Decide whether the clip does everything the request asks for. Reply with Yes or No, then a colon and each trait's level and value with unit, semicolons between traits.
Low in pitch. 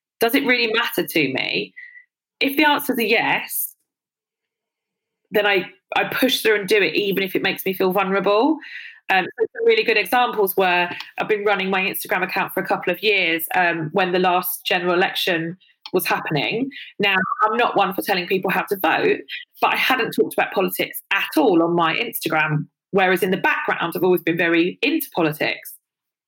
No: high, 195 Hz